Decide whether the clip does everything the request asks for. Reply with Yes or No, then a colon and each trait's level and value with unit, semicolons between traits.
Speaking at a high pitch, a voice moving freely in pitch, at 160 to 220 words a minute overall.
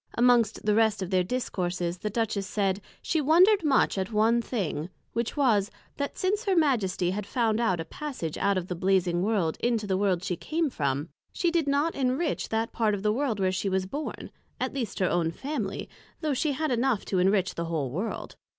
Yes: high, 210 Hz; wide, 6.1 semitones; fast, 205 wpm